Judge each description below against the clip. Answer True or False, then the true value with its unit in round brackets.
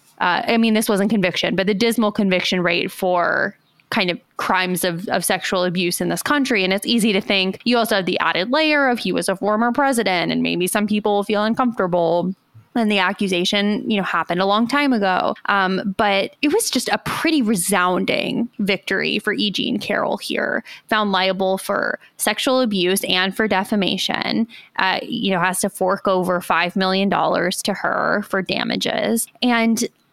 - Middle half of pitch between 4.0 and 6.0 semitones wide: False (3.5 semitones)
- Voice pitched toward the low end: False (200 Hz)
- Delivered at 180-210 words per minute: True (185 wpm)